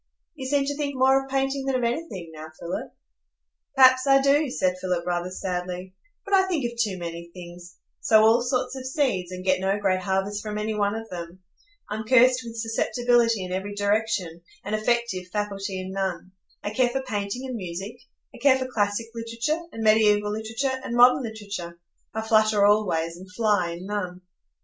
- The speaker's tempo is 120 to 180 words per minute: No, average, 190 wpm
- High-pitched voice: Yes, high, 215 Hz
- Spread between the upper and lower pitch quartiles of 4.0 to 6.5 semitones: Yes, average, 5.1 semitones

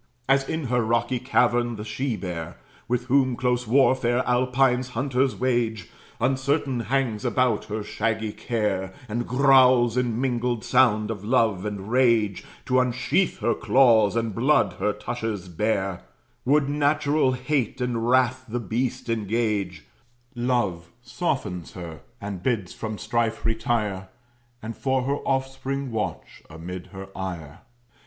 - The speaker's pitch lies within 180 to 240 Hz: No, low, 120 Hz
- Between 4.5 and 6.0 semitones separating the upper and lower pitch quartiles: No, average, 3.5 semitones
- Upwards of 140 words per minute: No, slow, 135 wpm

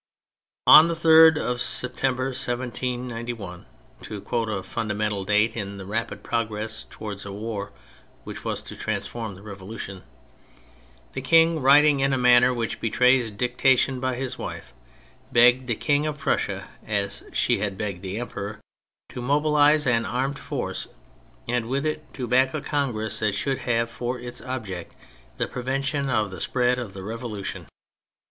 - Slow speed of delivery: No, average, 160 wpm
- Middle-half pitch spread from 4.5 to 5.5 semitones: No, average, 3.8 semitones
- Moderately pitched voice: No, low, 120 Hz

